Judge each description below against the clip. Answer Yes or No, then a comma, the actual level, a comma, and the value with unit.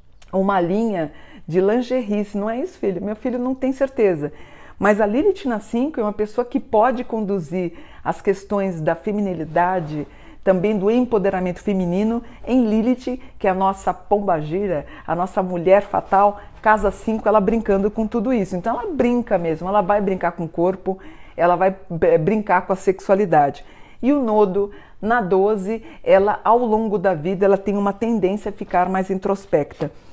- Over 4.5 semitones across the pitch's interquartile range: No, average, 2.8 semitones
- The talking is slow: No, average, 165 wpm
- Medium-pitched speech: No, high, 205 Hz